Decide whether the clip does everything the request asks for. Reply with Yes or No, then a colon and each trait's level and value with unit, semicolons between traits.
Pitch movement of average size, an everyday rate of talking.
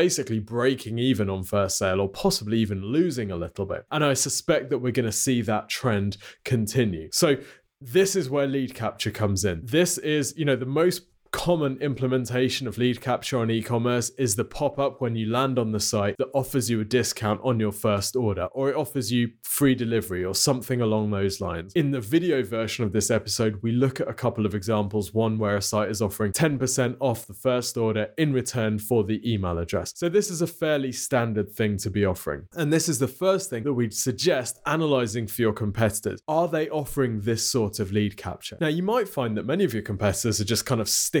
No: average, 4.3 semitones; fast, 220 wpm